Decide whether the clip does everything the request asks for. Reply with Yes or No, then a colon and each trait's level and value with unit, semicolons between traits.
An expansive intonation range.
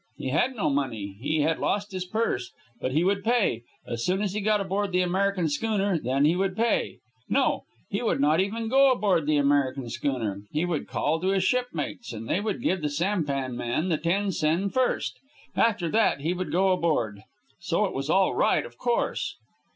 Yes: wide, 5.9 semitones